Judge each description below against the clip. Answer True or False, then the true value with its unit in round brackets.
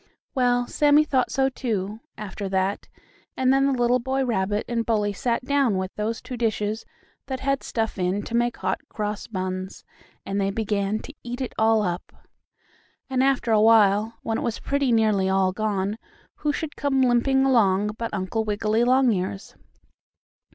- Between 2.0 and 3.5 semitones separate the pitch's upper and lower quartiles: False (4.0 semitones)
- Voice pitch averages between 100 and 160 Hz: False (225 Hz)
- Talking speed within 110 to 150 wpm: False (165 wpm)